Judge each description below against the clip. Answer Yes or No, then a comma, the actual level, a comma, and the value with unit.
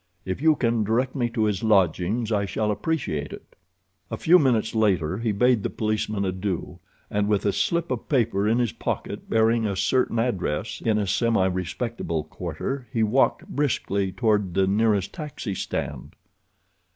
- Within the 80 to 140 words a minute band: No, average, 165 wpm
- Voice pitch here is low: Yes, low, 110 Hz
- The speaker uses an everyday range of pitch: Yes, average, 3.5 semitones